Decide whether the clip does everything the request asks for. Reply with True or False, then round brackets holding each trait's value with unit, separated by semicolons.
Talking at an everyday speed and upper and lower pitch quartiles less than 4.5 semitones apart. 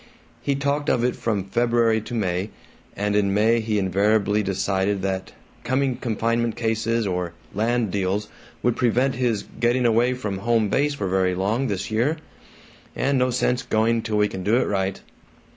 True (170 wpm; 3.5 semitones)